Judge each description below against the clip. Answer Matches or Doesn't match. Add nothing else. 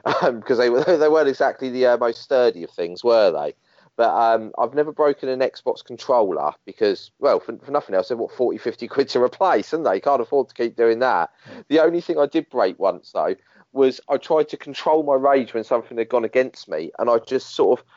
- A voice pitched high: Doesn't match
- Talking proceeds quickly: Matches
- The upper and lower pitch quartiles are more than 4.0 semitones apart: Matches